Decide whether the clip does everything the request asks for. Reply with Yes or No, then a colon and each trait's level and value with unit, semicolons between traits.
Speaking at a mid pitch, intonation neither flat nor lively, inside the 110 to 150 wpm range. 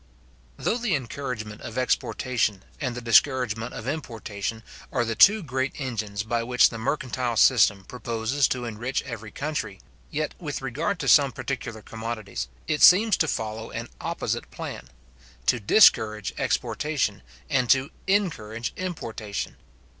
No: low, 120 Hz; average, 4.0 semitones; average, 140 wpm